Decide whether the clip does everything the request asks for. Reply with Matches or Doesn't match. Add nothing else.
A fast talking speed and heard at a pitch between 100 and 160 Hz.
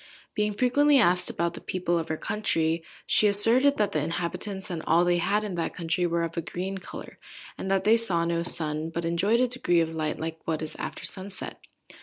Doesn't match